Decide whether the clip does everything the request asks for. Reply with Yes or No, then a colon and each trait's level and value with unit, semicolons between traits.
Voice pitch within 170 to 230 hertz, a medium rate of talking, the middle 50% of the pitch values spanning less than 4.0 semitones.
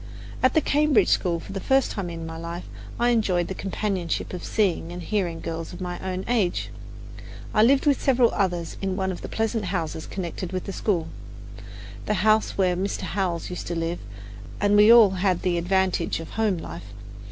Yes: high, 190 Hz; average, 195 wpm; average, 3.5 semitones